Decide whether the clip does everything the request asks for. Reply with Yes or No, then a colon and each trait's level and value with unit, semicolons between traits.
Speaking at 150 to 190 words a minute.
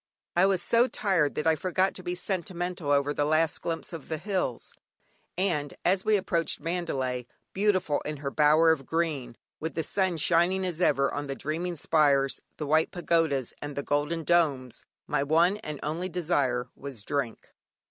Yes: average, 175 wpm